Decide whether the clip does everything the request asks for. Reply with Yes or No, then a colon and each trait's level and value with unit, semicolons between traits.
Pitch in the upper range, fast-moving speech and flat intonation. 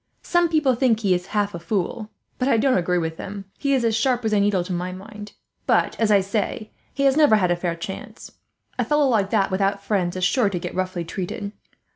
No: high, 205 Hz; fast, 235 wpm; average, 4.0 semitones